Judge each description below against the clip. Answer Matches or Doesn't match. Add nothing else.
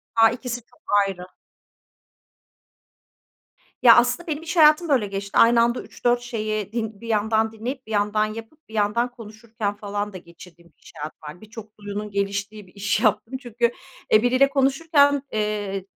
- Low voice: Doesn't match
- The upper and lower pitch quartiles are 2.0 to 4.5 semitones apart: Matches